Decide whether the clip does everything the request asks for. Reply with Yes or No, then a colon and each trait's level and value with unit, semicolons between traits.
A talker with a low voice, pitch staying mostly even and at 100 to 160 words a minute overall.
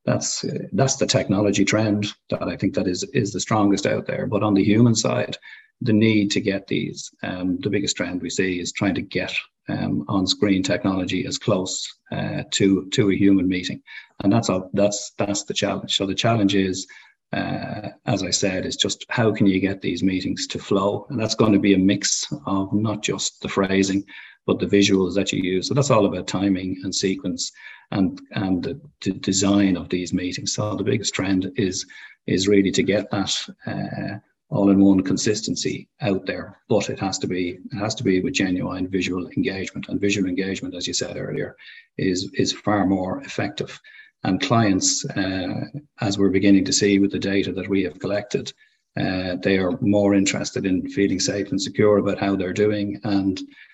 No: low, 100 Hz; narrow, 1.9 semitones; average, 195 wpm